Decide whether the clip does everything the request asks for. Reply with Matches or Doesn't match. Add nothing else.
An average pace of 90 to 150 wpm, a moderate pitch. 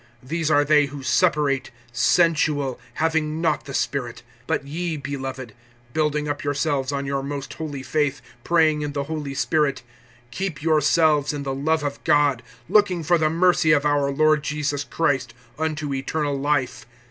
Doesn't match